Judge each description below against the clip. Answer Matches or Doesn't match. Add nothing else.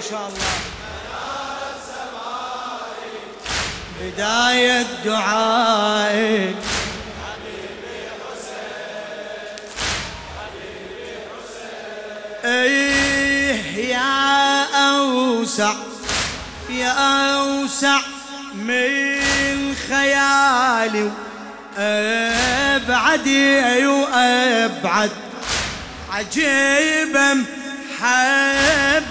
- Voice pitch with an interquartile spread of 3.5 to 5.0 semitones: Matches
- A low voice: Doesn't match